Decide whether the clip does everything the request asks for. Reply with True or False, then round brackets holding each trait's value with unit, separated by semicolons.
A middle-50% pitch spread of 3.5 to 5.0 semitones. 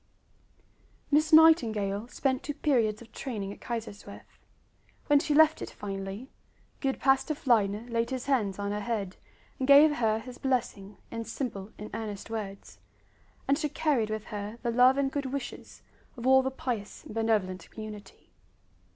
True (4.4 semitones)